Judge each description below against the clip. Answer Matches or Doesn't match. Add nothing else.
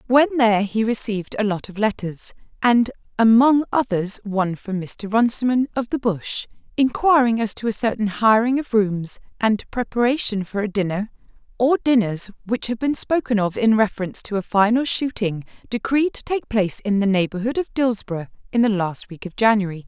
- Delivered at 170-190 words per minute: Matches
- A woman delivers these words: Matches